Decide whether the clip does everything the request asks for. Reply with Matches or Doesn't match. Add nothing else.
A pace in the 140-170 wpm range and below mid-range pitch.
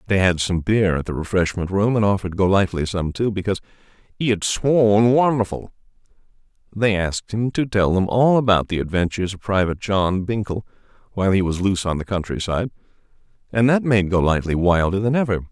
Doesn't match